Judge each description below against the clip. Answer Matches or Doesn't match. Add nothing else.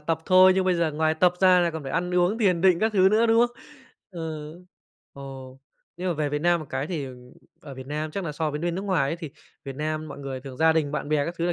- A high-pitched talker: Doesn't match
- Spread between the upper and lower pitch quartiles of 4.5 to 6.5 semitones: Doesn't match